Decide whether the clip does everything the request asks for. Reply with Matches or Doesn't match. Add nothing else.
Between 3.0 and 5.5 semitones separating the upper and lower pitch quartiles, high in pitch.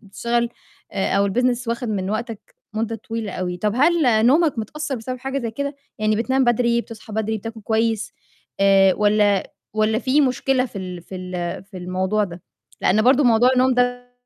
Matches